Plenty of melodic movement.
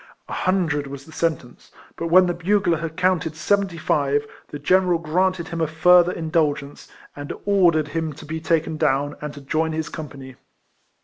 No: average, 3.0 semitones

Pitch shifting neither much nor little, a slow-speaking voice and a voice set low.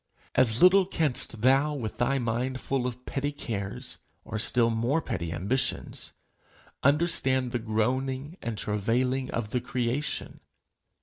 Yes: average, 3.0 semitones; slow, 130 wpm; low, 125 Hz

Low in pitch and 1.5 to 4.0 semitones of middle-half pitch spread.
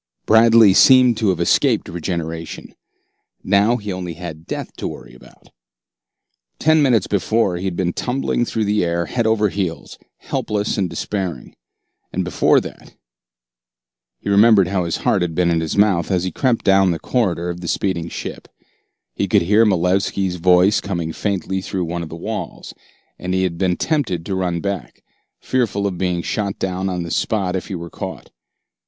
Yes: very low, 95 Hz; average, 3.2 semitones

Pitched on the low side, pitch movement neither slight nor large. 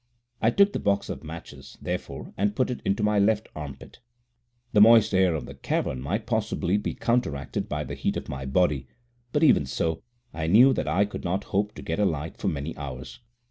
No: very low, 95 Hz; wide, 5.9 semitones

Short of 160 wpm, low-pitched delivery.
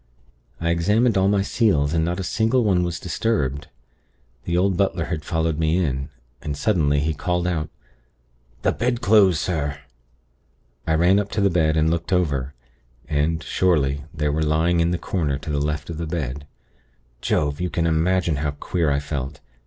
No: average, 175 wpm; very low, 80 Hz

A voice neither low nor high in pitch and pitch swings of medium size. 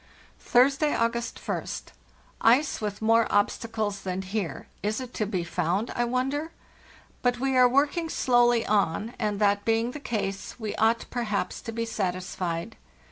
No: high, 225 Hz; average, 3.3 semitones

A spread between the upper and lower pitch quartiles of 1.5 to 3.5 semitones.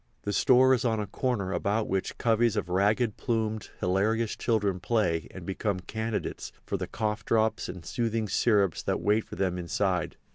Yes: average, 2.8 semitones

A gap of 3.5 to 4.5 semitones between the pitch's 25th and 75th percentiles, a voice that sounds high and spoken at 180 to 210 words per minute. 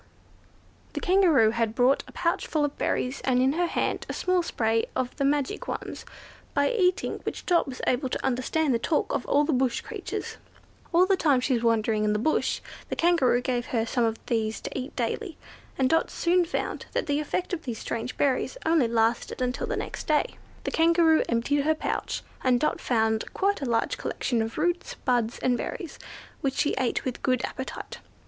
No: average, 5.3 semitones; very high, 265 Hz; average, 200 wpm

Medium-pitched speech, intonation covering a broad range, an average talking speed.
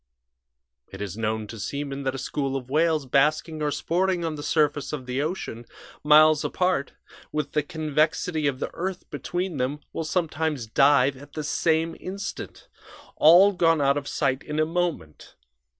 No: medium, 150 Hz; average, 3.0 semitones; average, 165 wpm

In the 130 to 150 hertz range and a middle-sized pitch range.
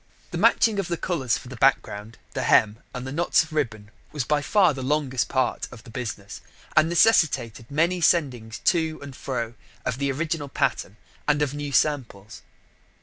Yes: medium, 140 Hz; average, 4.8 semitones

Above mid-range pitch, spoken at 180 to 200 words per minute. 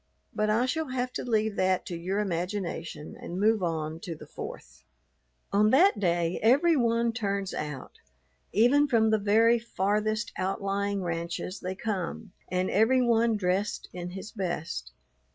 No: high, 200 Hz; average, 150 wpm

